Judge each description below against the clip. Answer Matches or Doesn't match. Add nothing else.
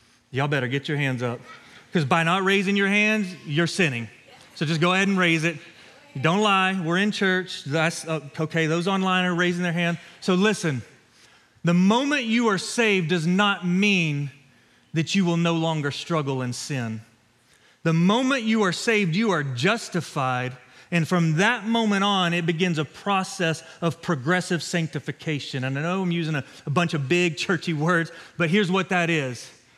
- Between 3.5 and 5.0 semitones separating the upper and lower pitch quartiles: Matches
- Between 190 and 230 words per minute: Doesn't match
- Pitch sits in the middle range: Matches